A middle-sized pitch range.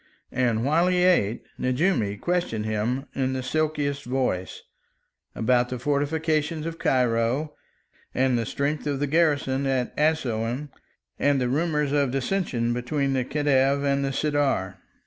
Yes: average, 3.3 semitones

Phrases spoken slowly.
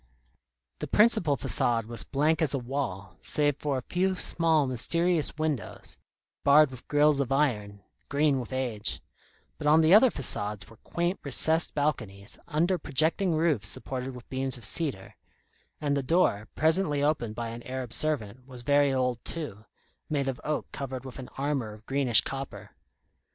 No: average, 160 wpm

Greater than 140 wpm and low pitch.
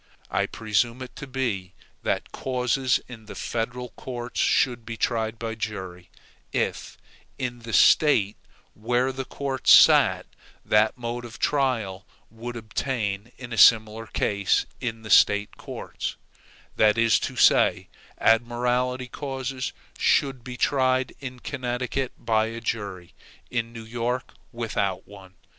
No: slow, 135 wpm; low, 120 Hz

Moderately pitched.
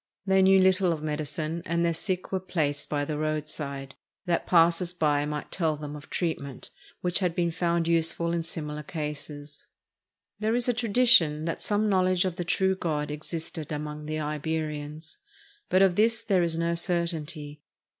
Yes: medium, 165 Hz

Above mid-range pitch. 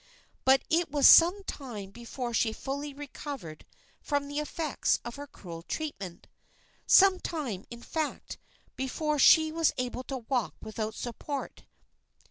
Yes: very high, 275 Hz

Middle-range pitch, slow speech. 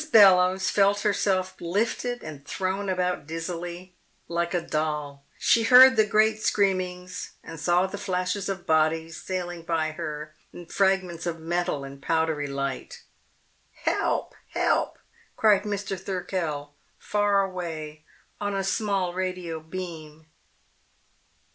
Yes: medium, 180 Hz; slow, 125 wpm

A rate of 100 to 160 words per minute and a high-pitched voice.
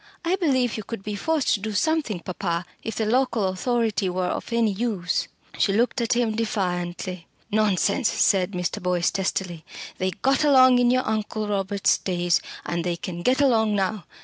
No: average, 175 wpm; high, 210 Hz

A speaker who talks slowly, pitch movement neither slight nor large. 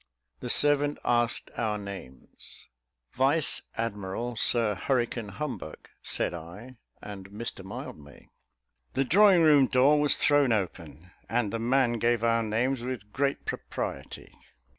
Yes: slow, 125 wpm; average, 4.6 semitones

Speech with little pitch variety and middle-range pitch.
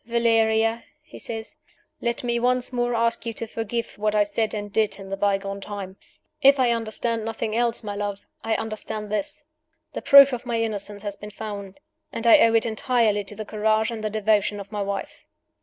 No: narrow, 2.1 semitones; high, 220 Hz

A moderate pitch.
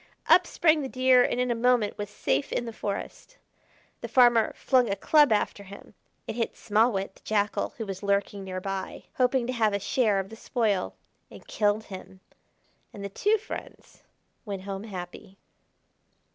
No: high, 215 Hz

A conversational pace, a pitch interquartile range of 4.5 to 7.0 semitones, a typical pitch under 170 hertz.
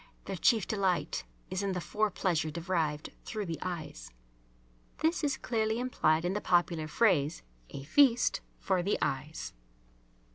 No: average, 145 wpm; wide, 5.4 semitones; medium, 185 Hz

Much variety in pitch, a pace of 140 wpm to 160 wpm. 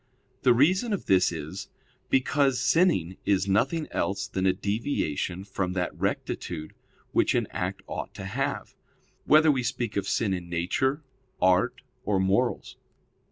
Yes: wide, 6.4 semitones; average, 145 wpm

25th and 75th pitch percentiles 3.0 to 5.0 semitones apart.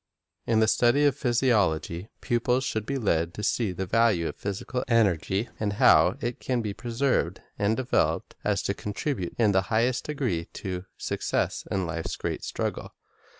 Yes: average, 4.5 semitones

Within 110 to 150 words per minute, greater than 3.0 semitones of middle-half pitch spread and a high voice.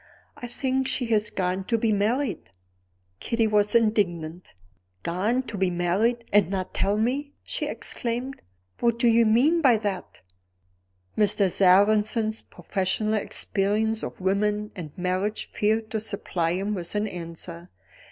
Yes: average, 140 wpm; average, 3.4 semitones; high, 210 Hz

